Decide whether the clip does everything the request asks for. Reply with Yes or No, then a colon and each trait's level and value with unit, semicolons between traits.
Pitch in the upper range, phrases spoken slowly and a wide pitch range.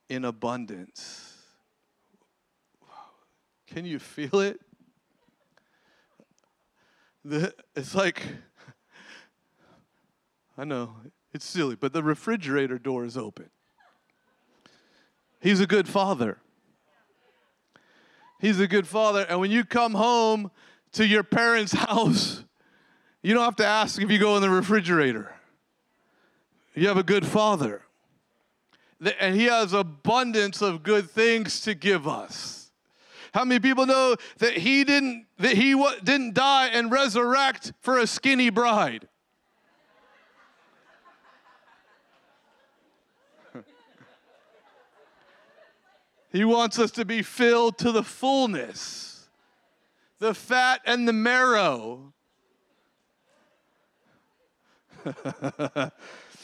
No: high, 215 Hz; slow, 100 wpm; average, 4.4 semitones